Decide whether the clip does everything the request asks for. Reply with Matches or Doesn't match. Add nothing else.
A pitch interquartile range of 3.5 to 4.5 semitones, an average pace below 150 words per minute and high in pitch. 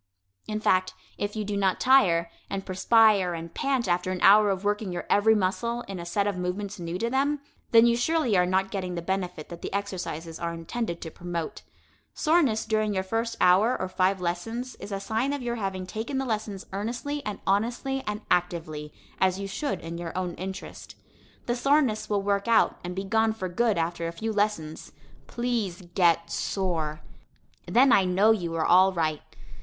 Doesn't match